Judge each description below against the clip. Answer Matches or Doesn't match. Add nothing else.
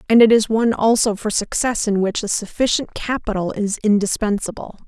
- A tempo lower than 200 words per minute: Matches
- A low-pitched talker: Doesn't match